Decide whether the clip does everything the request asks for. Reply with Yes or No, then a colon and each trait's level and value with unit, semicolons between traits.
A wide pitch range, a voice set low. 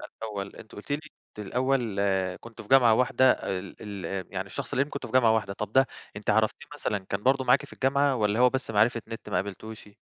No: average, 4.2 semitones; low, 110 Hz